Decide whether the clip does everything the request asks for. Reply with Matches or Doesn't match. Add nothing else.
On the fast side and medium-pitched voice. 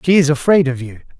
Matches